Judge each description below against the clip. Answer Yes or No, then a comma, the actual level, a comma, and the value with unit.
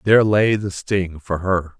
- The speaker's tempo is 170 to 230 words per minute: Yes, average, 200 wpm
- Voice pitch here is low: Yes, very low, 95 Hz